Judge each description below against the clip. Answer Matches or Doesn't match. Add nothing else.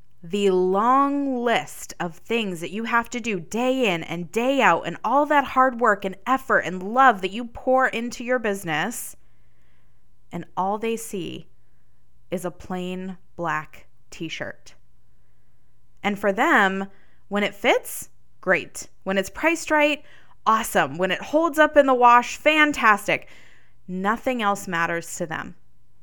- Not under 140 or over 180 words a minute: Matches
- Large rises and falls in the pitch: Matches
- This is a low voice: Doesn't match